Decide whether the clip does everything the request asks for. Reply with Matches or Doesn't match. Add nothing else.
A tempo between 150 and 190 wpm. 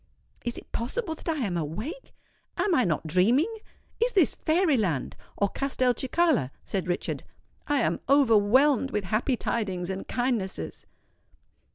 Doesn't match